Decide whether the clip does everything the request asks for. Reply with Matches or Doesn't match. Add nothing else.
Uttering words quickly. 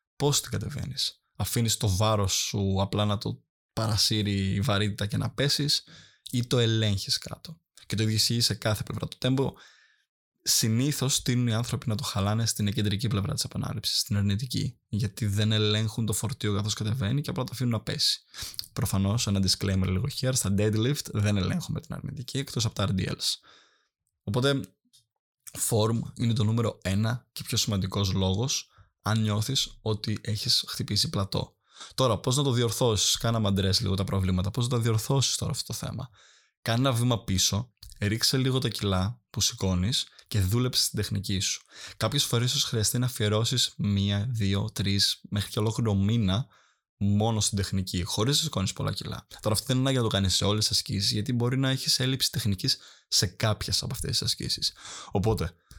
Matches